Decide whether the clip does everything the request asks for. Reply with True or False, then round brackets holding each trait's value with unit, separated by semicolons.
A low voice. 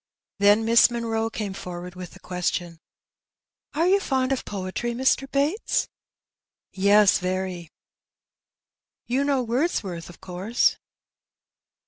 False (210 Hz)